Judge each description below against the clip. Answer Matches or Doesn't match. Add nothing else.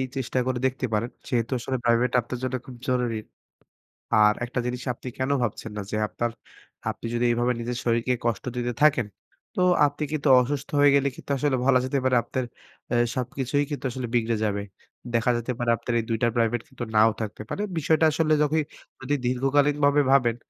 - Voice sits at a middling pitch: Doesn't match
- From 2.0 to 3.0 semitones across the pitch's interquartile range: Matches